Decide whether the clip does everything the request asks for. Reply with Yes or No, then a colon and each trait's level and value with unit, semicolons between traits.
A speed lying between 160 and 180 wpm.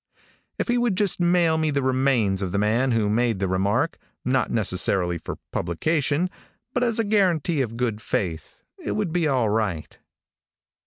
Yes: average, 170 wpm